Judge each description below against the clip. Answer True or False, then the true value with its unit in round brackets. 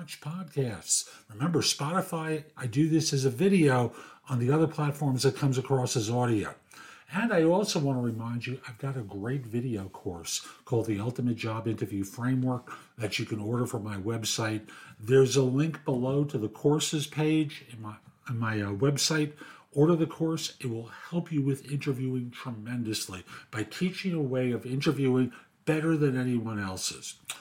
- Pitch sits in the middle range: False (130 Hz)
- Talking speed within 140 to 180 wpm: True (170 wpm)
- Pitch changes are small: False (4.3 semitones)